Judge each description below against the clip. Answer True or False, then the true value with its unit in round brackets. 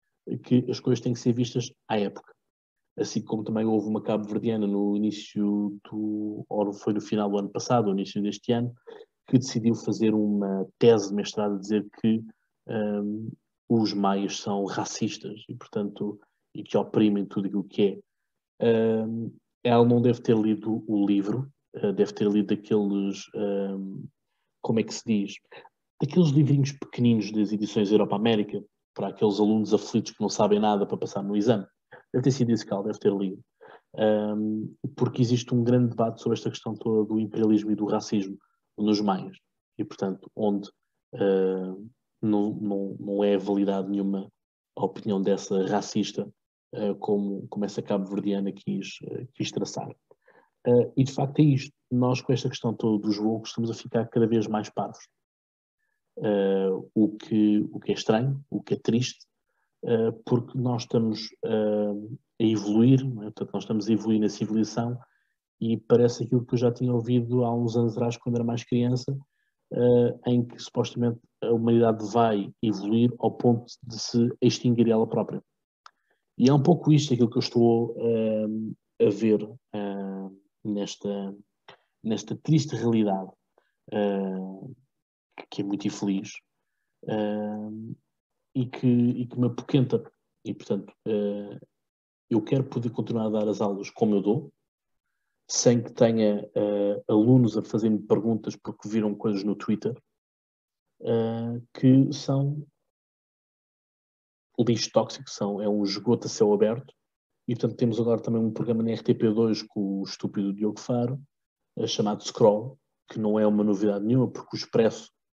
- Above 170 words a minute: False (155 wpm)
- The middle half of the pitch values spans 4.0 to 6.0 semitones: False (2.7 semitones)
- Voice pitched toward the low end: True (110 Hz)